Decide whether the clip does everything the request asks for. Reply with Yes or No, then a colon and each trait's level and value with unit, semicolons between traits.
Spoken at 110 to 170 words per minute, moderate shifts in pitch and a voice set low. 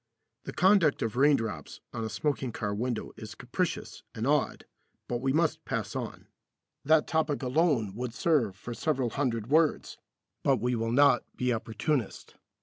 Yes: average, 155 wpm; average, 4.8 semitones; low, 125 Hz